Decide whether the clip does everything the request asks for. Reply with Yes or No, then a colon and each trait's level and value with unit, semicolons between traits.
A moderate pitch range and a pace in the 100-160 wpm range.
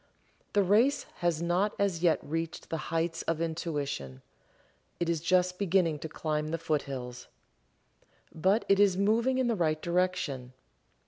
Yes: average, 3.5 semitones; average, 145 wpm